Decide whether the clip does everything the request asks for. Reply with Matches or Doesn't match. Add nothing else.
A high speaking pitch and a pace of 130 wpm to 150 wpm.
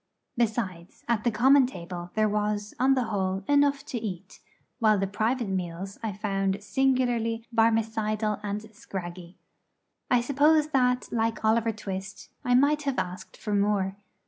Matches